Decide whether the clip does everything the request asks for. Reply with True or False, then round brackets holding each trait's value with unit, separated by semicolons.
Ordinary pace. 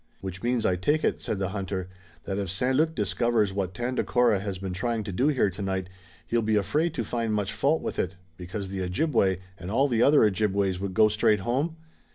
False (210 wpm)